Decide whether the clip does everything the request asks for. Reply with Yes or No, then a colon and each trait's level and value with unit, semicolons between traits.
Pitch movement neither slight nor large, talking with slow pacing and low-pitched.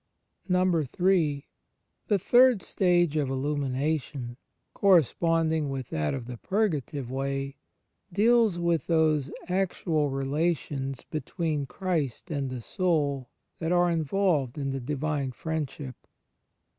No: average, 4.3 semitones; slow, 105 wpm; medium, 155 Hz